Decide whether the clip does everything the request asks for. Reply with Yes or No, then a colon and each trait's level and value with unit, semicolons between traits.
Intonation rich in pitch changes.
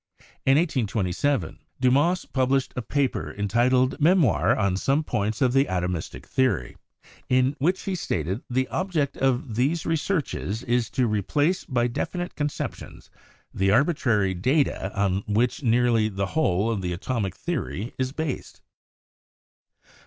Yes: wide, 5.8 semitones